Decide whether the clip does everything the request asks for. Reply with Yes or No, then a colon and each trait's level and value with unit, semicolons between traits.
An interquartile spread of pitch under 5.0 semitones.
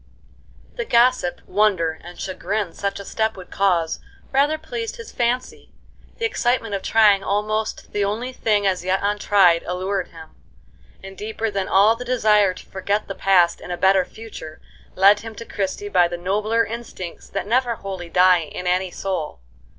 Yes: average, 3.4 semitones